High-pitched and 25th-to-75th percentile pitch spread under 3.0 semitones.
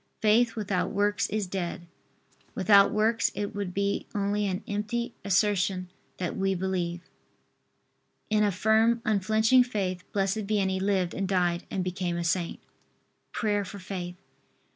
Yes: high, 200 Hz; narrow, 2.4 semitones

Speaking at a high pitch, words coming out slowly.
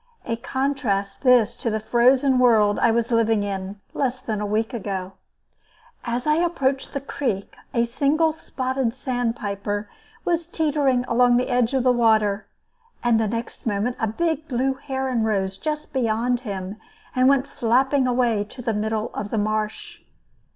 No: high, 240 Hz; average, 160 wpm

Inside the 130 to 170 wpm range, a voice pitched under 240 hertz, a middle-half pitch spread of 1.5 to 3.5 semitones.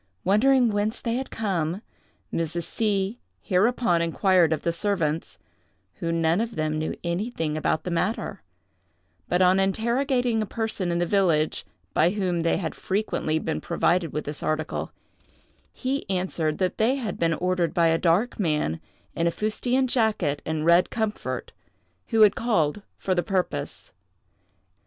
No: average, 150 wpm; medium, 185 Hz; average, 4.8 semitones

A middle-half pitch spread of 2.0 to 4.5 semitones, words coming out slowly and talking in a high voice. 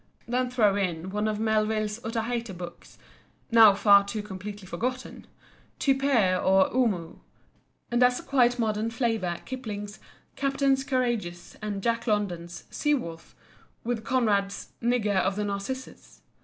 Yes: average, 3.6 semitones; slow, 125 wpm; high, 215 Hz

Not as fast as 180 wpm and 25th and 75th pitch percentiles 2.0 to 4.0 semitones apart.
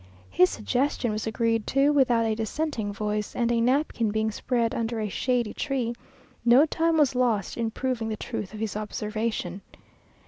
Yes: average, 170 wpm; average, 2.9 semitones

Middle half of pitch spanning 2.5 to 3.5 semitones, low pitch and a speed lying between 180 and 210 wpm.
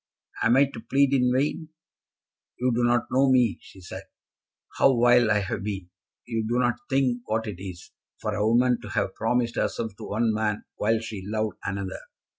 Yes: average, 2.9 semitones; low, 115 Hz; average, 190 wpm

